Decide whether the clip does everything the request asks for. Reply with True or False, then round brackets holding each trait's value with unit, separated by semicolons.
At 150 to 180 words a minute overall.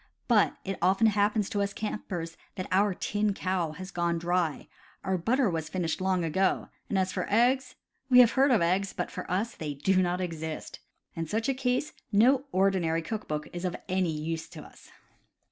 False (195 wpm)